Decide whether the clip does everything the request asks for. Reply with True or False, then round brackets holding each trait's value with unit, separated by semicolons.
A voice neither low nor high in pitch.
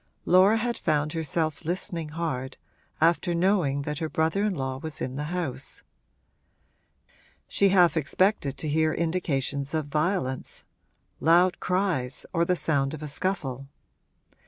True (160 Hz)